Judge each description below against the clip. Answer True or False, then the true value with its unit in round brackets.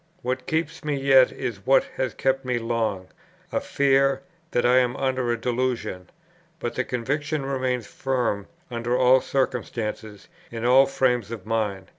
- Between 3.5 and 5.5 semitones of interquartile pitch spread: False (2.4 semitones)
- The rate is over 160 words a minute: False (155 wpm)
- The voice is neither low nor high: False (125 Hz)